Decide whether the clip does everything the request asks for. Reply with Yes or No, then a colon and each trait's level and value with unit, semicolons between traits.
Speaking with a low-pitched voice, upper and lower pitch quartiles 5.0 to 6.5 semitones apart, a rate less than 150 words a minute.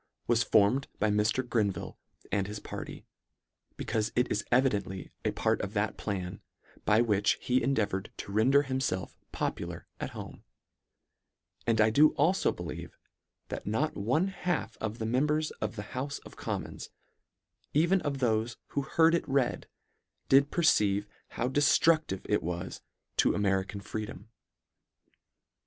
Yes: low, 115 Hz; wide, 5.4 semitones; average, 140 wpm